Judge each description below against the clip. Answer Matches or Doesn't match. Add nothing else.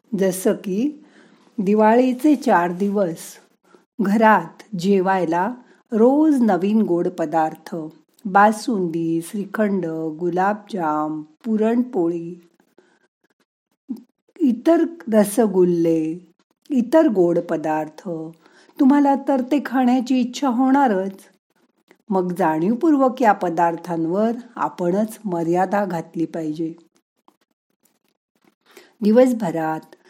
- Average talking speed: Doesn't match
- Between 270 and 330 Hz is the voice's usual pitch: Doesn't match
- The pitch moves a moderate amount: Doesn't match